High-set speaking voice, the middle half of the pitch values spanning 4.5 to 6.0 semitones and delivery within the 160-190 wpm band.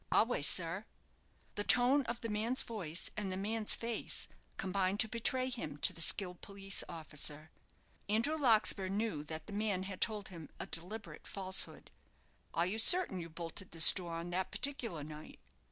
Yes: high, 195 Hz; average, 4.9 semitones; average, 170 wpm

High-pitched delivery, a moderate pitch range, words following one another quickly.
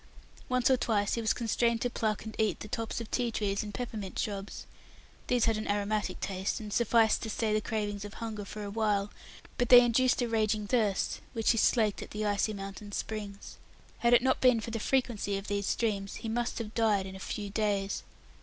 No: high, 215 Hz; narrow, 2.1 semitones; fast, 215 wpm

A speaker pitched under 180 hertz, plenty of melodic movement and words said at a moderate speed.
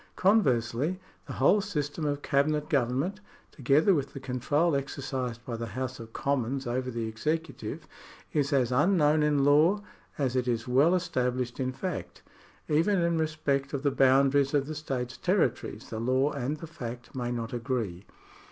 No: medium, 140 Hz; average, 3.7 semitones; average, 160 wpm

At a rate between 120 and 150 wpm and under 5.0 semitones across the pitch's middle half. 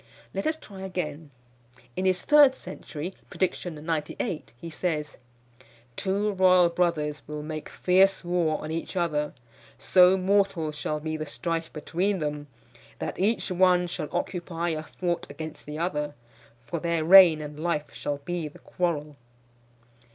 Yes: average, 145 wpm; average, 3.3 semitones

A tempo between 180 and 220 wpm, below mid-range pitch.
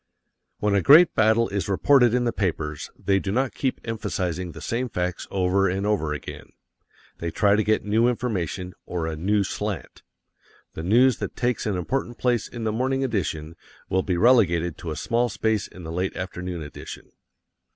Yes: average, 185 wpm; low, 100 Hz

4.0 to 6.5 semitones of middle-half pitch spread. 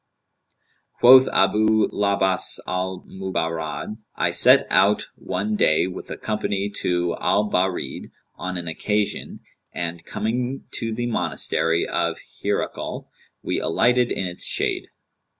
No: average, 3.6 semitones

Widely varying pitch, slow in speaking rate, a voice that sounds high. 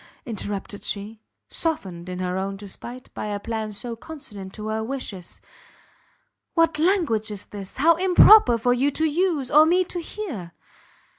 No: wide, 7.7 semitones; average, 155 wpm; high, 230 Hz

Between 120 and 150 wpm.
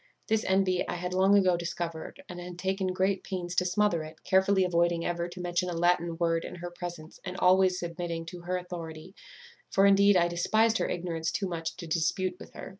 No: fast, 205 wpm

